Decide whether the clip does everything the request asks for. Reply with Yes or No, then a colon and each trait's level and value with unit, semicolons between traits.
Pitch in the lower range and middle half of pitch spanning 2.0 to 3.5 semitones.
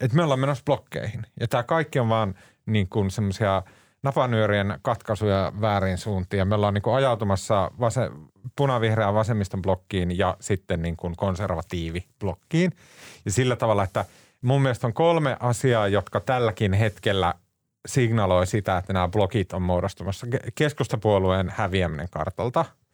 No: low, 105 Hz; average, 4.4 semitones